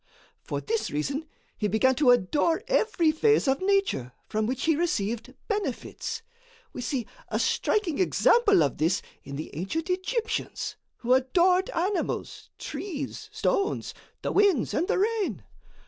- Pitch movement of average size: No, wide, 8.3 semitones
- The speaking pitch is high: Yes, very high, 320 Hz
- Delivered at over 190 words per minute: No, average, 140 wpm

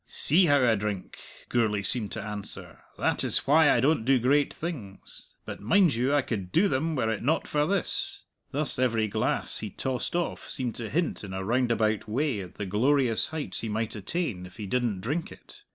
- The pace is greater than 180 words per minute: Yes, average, 200 wpm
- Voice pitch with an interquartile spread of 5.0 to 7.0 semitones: Yes, wide, 5.5 semitones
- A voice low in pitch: Yes, low, 120 Hz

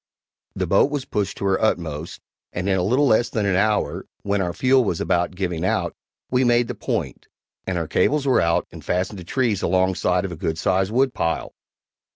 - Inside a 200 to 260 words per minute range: Yes, fast, 205 wpm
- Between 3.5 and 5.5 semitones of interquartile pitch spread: Yes, average, 5.1 semitones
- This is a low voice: Yes, very low, 95 Hz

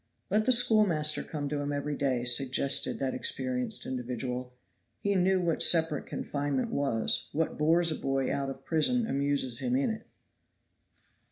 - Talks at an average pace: Yes, average, 155 wpm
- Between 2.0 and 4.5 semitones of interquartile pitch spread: Yes, average, 4.1 semitones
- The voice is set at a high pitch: No, medium, 145 Hz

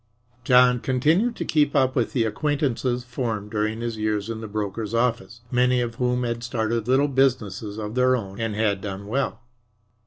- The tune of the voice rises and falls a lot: No, average, 2.8 semitones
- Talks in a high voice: No, low, 120 Hz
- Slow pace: No, average, 180 wpm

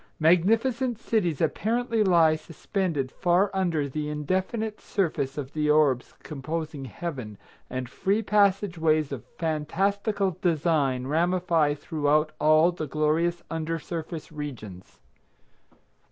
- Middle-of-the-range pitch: Yes, medium, 160 Hz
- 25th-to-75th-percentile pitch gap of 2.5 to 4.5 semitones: Yes, average, 3.9 semitones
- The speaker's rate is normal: No, slow, 110 wpm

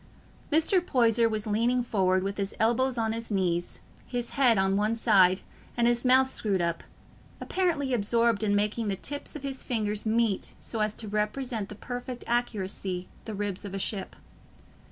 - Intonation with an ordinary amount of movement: Yes, average, 3.3 semitones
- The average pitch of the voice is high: Yes, high, 220 Hz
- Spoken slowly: No, average, 170 wpm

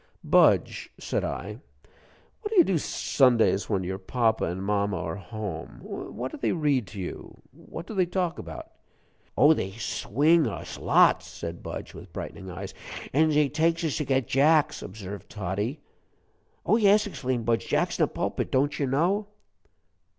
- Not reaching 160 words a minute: No, average, 165 wpm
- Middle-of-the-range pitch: No, low, 130 Hz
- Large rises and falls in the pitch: Yes, wide, 8.0 semitones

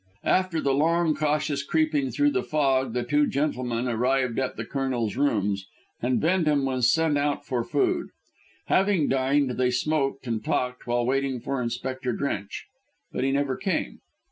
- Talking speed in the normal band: Yes, average, 160 wpm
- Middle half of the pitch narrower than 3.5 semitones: Yes, average, 3.0 semitones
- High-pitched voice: No, low, 135 Hz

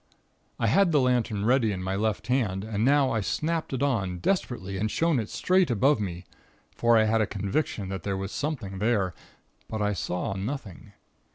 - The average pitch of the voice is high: No, low, 110 Hz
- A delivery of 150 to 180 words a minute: No, average, 190 wpm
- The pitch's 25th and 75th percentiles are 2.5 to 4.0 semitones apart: No, average, 5.2 semitones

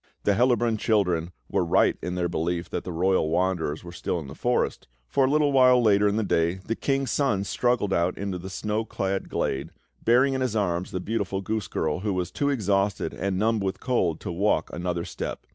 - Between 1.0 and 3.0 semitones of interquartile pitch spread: No, average, 4.3 semitones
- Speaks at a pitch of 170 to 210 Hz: No, low, 100 Hz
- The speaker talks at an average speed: No, fast, 210 wpm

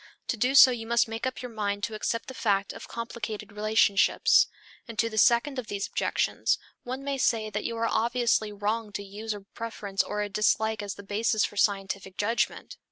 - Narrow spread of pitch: Yes, narrow, 2.2 semitones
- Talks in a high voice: Yes, high, 220 Hz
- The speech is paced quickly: Yes, fast, 210 wpm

